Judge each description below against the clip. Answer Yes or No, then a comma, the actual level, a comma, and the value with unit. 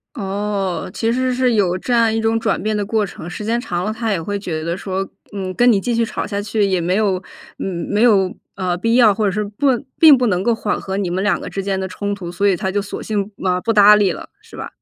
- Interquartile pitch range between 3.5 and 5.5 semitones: No, average, 2.9 semitones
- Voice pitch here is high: Yes, high, 205 Hz